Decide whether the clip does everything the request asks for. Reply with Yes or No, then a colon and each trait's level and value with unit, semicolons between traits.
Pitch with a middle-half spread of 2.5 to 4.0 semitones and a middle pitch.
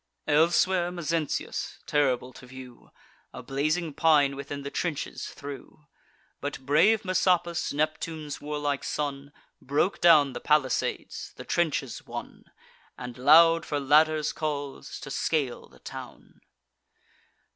Yes: average, 2.8 semitones; medium, 150 Hz